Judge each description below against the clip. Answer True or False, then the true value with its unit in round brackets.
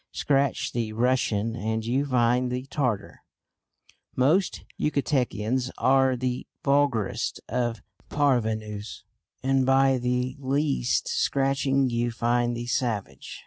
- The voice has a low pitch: True (125 Hz)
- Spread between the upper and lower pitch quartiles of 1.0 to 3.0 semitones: True (2.5 semitones)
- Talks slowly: True (105 wpm)